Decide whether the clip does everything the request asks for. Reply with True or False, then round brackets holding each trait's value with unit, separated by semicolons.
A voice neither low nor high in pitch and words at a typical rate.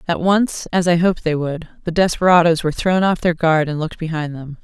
False (165 Hz; 235 wpm)